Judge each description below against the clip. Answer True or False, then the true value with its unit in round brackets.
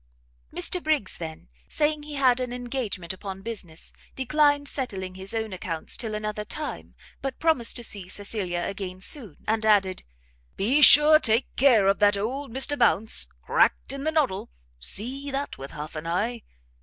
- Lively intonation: True (6.2 semitones)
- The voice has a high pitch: True (225 Hz)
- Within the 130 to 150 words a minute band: False (165 wpm)